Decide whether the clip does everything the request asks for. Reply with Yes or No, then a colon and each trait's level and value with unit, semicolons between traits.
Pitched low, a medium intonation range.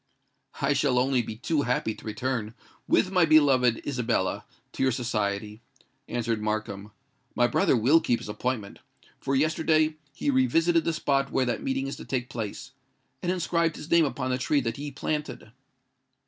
Yes: low, 130 Hz; average, 4.4 semitones